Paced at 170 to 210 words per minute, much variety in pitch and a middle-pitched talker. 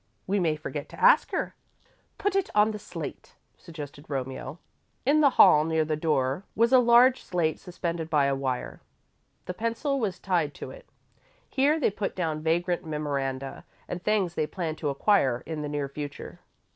Yes: average, 175 wpm; wide, 6.2 semitones; medium, 165 Hz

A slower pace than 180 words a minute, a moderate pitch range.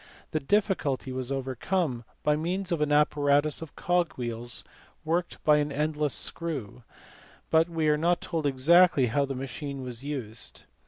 Yes: average, 150 wpm; average, 3.8 semitones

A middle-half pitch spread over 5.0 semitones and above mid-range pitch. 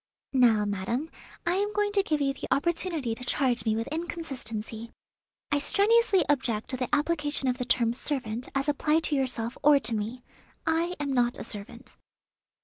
Yes: wide, 5.4 semitones; very high, 270 Hz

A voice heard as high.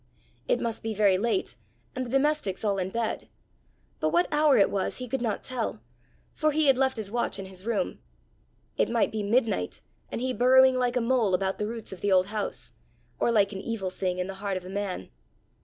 Yes: high, 220 Hz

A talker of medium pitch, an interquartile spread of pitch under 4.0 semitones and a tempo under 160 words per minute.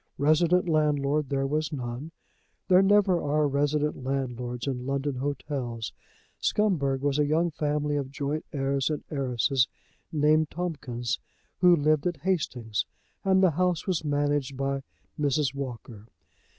Yes: medium, 145 Hz; narrow, 2.4 semitones; slow, 135 wpm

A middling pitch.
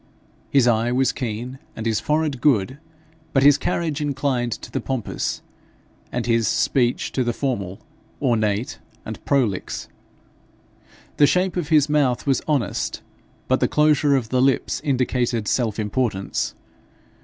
No: low, 130 Hz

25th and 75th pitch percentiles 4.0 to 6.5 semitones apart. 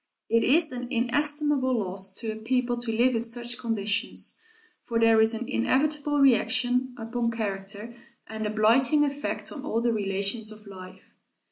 No: average, 3.0 semitones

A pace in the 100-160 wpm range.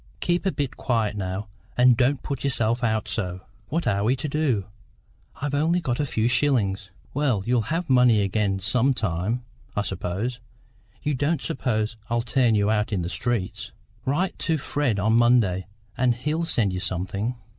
No: average, 175 wpm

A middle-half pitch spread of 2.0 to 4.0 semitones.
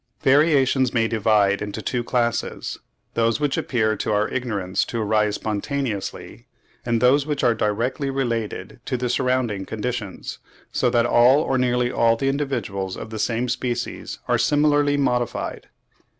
Yes: average, 3.3 semitones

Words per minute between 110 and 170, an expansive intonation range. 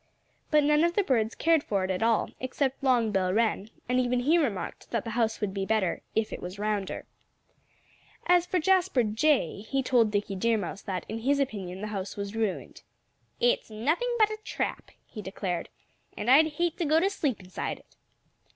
No: average, 195 wpm; wide, 6.7 semitones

